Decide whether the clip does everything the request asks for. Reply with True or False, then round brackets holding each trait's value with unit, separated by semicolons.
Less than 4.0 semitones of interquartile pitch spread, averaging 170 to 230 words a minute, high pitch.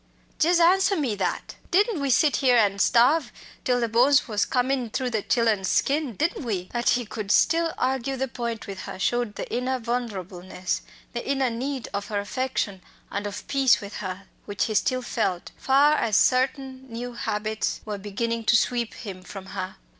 False (4.4 semitones; 185 wpm; 235 Hz)